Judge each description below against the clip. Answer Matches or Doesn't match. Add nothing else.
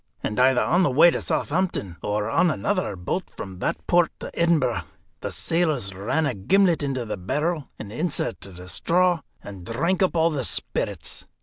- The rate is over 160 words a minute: Matches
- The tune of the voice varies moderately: Doesn't match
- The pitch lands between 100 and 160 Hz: Matches